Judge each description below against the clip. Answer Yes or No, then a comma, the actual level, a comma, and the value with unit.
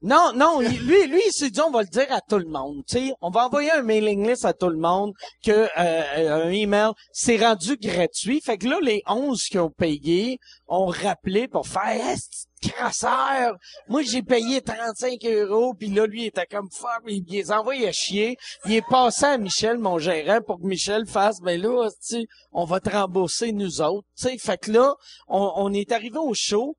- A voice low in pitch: No, high, 215 Hz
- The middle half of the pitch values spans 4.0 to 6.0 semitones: Yes, average, 4.6 semitones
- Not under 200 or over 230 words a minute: Yes, average, 215 wpm